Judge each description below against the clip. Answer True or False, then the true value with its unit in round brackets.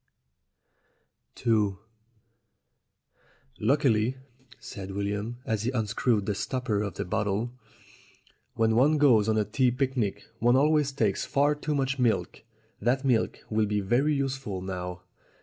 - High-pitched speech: False (115 Hz)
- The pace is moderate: False (130 wpm)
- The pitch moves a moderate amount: True (4.4 semitones)